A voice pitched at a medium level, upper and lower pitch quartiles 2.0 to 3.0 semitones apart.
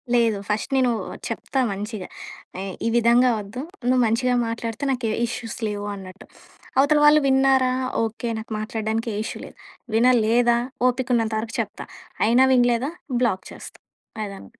No: high, 230 Hz; average, 2.7 semitones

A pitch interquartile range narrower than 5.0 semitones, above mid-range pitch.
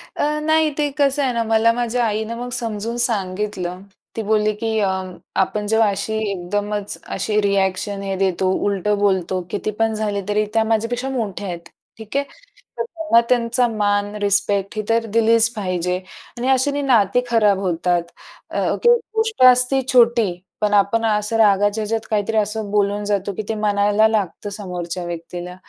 Yes: narrow, 2.5 semitones; high, 210 Hz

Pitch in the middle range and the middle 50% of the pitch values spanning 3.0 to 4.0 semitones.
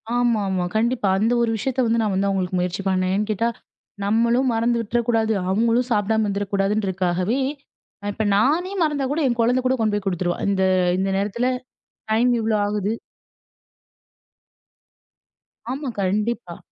No: high, 220 Hz; average, 3.4 semitones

